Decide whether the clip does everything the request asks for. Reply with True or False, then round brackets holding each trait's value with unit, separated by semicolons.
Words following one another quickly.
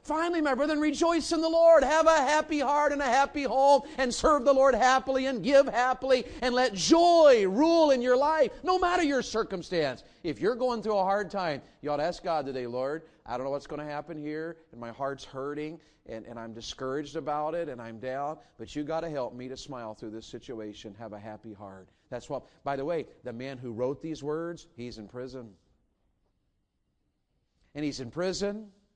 True (210 wpm)